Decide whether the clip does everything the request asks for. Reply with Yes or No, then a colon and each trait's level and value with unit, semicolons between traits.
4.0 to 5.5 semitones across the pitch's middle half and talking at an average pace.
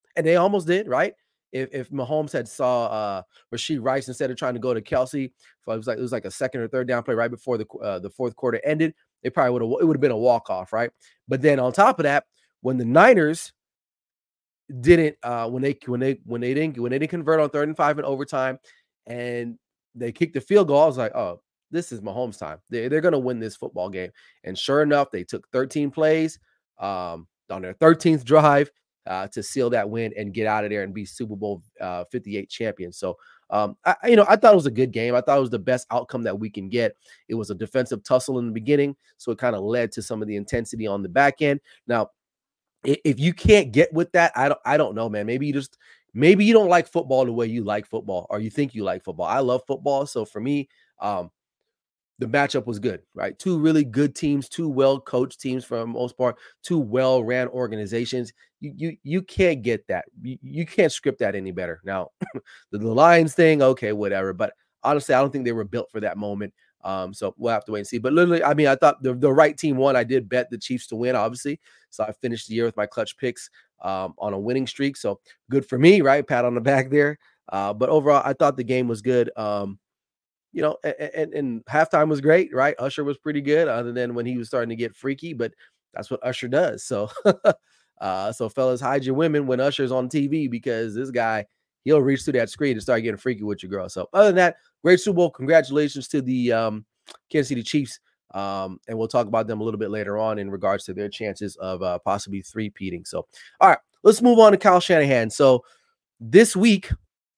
No: average, 4.5 semitones; fast, 235 wpm